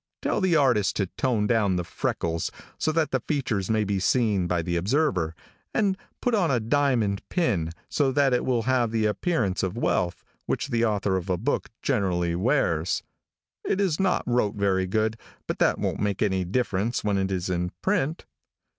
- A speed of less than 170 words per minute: No, average, 185 wpm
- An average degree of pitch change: No, wide, 6.0 semitones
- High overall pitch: No, low, 110 Hz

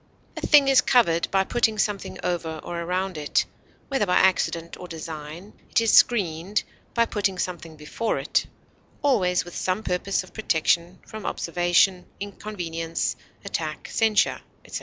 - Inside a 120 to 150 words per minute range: Yes, average, 145 wpm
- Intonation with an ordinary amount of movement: Yes, average, 4.0 semitones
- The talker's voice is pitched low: No, medium, 180 Hz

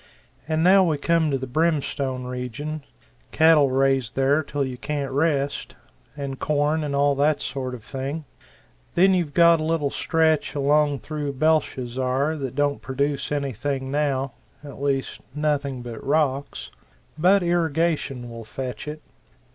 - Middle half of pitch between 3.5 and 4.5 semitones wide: No, average, 2.7 semitones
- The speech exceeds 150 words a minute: No, average, 145 wpm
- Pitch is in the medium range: Yes, medium, 145 Hz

